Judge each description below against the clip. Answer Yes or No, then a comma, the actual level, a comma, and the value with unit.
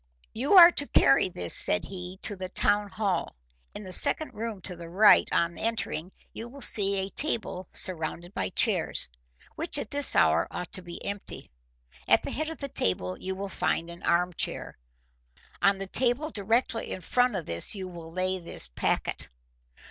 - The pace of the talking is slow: No, average, 185 wpm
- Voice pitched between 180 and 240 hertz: Yes, high, 190 Hz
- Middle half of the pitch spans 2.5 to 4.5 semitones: No, average, 4.9 semitones